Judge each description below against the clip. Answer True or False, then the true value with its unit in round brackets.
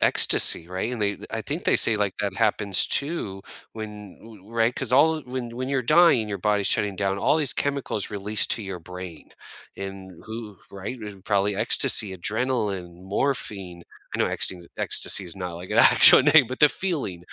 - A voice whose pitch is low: True (105 Hz)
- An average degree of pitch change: True (4.5 semitones)